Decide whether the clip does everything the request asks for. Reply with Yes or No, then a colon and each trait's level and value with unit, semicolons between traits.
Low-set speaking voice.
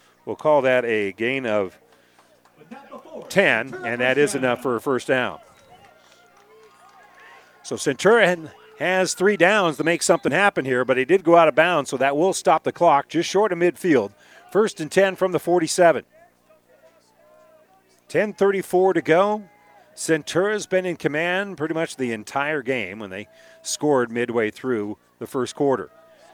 No: medium, 165 Hz